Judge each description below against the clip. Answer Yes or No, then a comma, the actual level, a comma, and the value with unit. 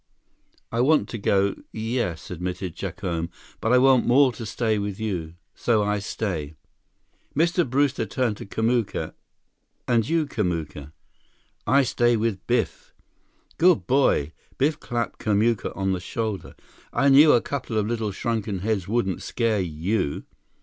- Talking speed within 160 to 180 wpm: No, average, 145 wpm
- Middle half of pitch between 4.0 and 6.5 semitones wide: Yes, average, 4.4 semitones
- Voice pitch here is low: Yes, low, 110 Hz